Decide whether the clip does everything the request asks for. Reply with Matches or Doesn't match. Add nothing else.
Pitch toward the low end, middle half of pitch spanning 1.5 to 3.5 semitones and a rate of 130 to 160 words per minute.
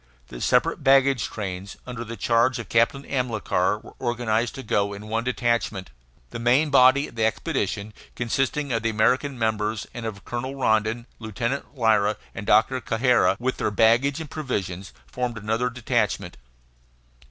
Matches